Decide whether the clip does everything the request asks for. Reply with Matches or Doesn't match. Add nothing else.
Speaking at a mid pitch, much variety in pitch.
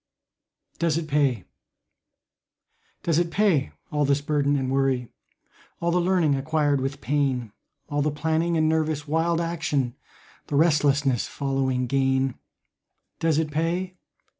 Doesn't match